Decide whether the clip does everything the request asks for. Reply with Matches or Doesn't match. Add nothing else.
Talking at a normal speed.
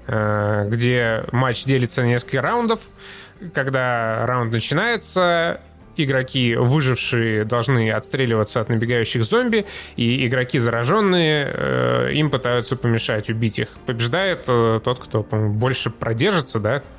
Doesn't match